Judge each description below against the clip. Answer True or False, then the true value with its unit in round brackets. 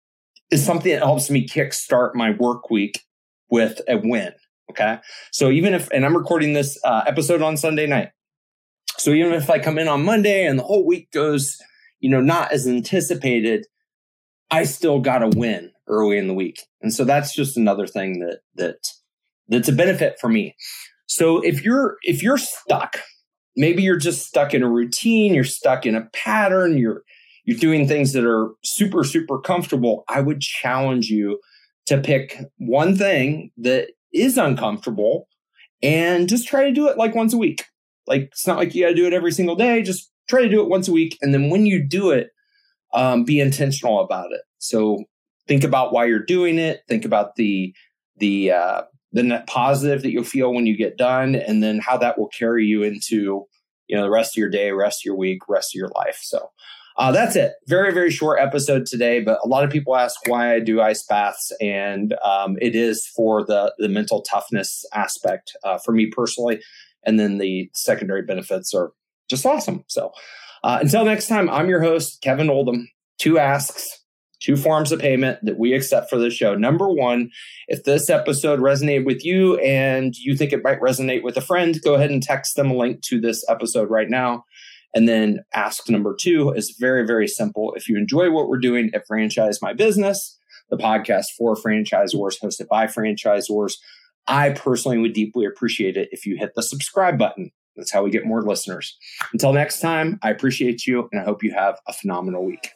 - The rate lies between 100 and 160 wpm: False (200 wpm)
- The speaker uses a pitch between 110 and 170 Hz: True (135 Hz)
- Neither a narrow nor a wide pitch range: False (6.9 semitones)